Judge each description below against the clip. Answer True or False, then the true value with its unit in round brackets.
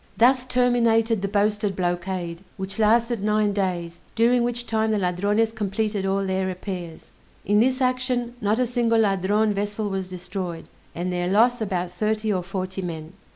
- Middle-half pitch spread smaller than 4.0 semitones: True (3.4 semitones)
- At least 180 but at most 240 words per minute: False (160 wpm)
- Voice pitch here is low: False (205 Hz)